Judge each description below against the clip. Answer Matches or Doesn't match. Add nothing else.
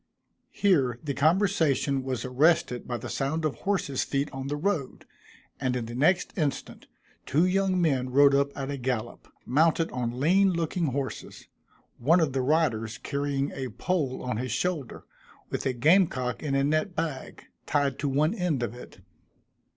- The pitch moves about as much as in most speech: Matches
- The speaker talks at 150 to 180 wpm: Matches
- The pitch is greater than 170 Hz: Doesn't match